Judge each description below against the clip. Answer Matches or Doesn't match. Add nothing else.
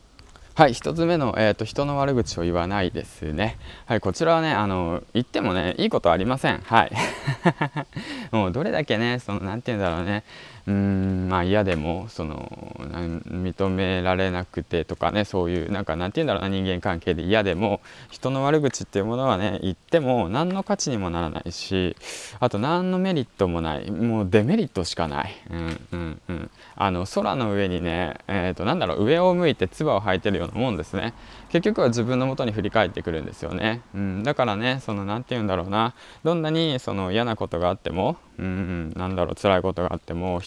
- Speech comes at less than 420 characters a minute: Matches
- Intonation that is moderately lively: Matches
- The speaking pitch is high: Doesn't match